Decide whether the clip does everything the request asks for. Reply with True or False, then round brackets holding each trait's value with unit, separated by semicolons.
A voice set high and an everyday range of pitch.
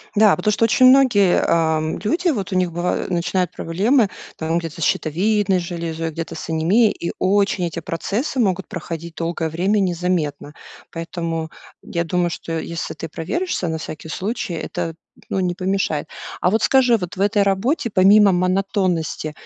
False (180 Hz; 3.5 semitones)